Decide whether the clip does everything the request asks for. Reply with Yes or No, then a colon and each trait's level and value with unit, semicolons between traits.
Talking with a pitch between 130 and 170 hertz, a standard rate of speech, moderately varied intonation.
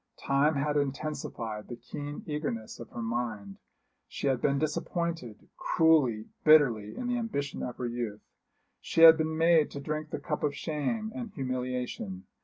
Yes: medium, 140 Hz; average, 160 wpm; average, 4.7 semitones